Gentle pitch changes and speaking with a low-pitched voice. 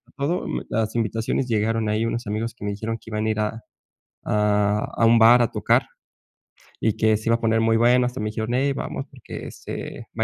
Yes: narrow, 1.5 semitones; low, 115 Hz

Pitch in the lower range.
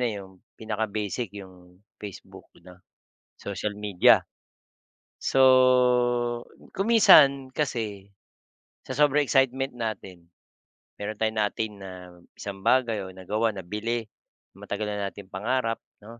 Yes: low, 105 Hz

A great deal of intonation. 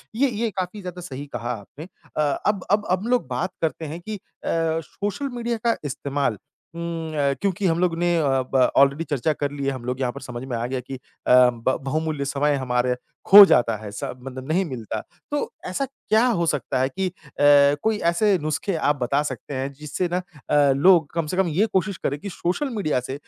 Yes: wide, 5.7 semitones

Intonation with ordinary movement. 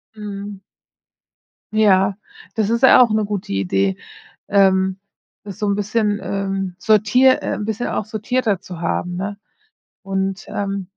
No: narrow, 1.9 semitones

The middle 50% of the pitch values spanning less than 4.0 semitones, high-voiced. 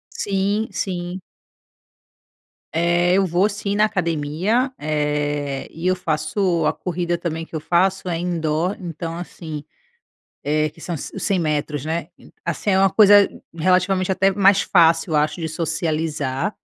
No: average, 3.5 semitones; medium, 170 Hz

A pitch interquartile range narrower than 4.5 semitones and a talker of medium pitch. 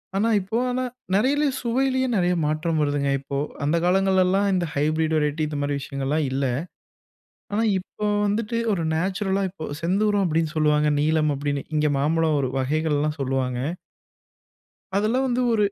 No: average, 5.1 semitones; medium, 160 Hz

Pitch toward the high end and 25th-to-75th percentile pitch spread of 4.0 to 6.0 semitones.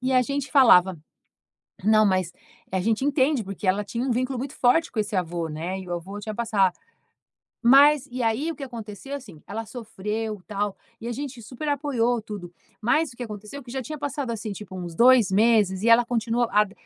Yes: high, 225 Hz; average, 4.3 semitones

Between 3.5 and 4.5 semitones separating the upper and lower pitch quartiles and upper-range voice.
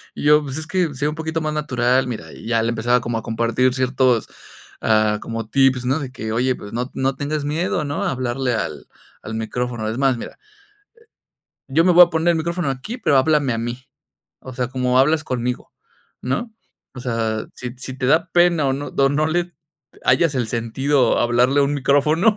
No: average, 4.0 semitones; low, 130 Hz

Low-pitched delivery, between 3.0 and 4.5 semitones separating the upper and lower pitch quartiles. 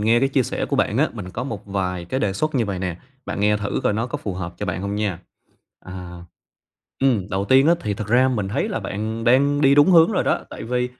No: low, 105 Hz; average, 5.2 semitones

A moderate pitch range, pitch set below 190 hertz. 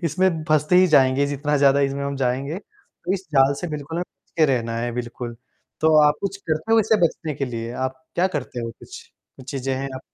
Yes: average, 3.3 semitones; medium, 140 Hz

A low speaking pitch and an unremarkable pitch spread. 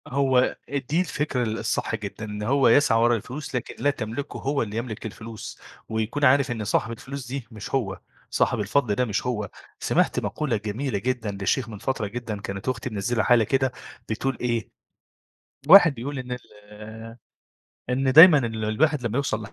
Yes: low, 120 Hz; average, 3.7 semitones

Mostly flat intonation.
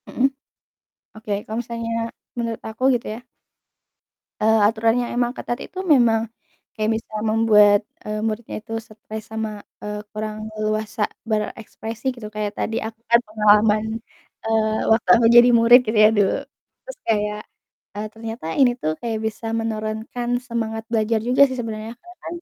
Yes: narrow, 1.5 semitones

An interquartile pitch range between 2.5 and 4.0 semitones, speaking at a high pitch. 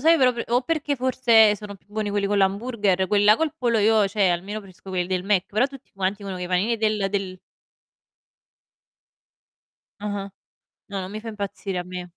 Yes: average, 2.8 semitones; high, 205 Hz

